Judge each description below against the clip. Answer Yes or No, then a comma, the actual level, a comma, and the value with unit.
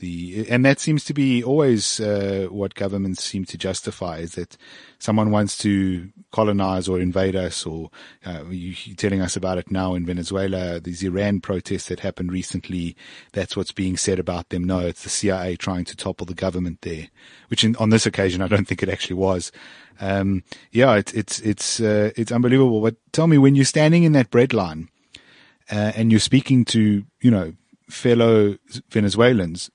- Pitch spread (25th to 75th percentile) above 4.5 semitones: No, average, 3.3 semitones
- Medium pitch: No, very low, 95 Hz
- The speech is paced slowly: No, average, 185 wpm